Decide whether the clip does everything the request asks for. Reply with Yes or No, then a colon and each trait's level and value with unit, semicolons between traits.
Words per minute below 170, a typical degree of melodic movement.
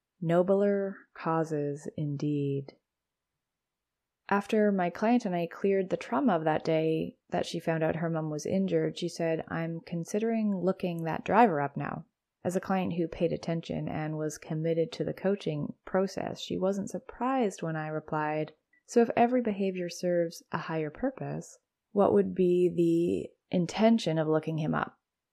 Yes: average, 160 wpm; average, 3.6 semitones